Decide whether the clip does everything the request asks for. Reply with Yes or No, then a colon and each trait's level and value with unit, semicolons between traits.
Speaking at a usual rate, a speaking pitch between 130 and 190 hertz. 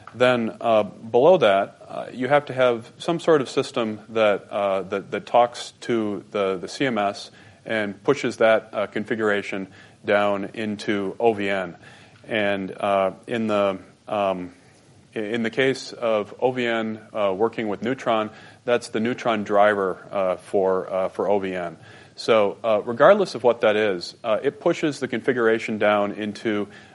No: average, 150 wpm; low, 110 Hz